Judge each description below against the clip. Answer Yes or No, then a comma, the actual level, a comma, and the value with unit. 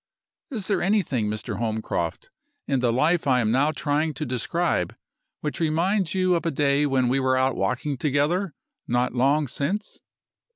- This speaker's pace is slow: No, average, 165 wpm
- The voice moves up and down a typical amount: Yes, average, 5.0 semitones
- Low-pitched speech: No, medium, 145 Hz